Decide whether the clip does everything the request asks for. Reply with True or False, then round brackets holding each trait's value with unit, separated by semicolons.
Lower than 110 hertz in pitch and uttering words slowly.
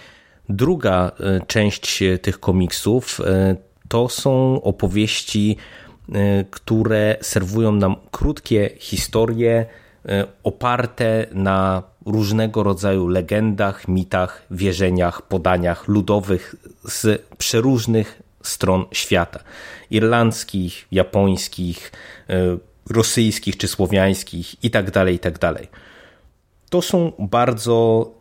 True (100 Hz; 75 wpm)